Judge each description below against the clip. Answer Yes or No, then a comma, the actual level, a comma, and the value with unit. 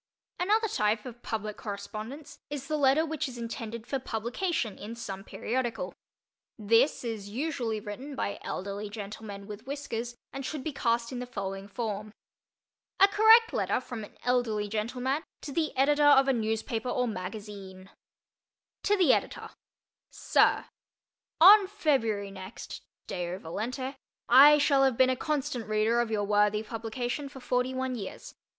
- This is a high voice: Yes, high, 235 Hz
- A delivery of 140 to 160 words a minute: Yes, average, 150 wpm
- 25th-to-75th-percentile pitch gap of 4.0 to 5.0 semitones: Yes, average, 4.4 semitones